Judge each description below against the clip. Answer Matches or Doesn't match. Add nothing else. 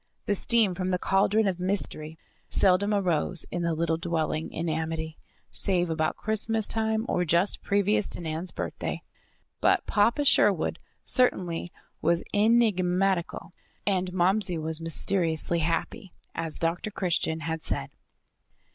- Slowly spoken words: Matches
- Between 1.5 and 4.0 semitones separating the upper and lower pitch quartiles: Matches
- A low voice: Doesn't match